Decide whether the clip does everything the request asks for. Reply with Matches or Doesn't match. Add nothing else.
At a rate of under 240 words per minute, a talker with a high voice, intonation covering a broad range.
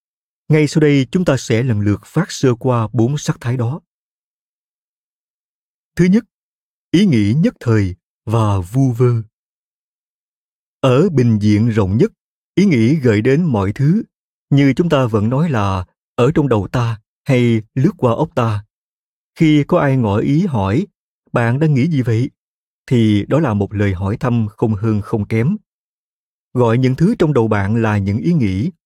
Doesn't match